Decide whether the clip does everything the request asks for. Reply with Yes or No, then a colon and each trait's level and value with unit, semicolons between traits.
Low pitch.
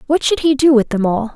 No: very high, 260 Hz